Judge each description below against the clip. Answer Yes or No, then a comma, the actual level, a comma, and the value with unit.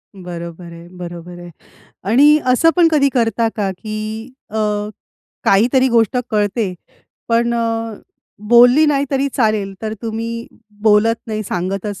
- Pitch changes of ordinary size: Yes, average, 3.4 semitones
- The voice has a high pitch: Yes, high, 225 Hz